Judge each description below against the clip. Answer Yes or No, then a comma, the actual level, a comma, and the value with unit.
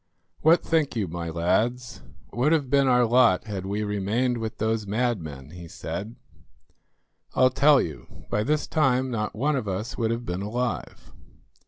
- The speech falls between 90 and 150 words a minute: No, average, 165 wpm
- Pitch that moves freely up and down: No, average, 4.3 semitones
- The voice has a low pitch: Yes, low, 115 Hz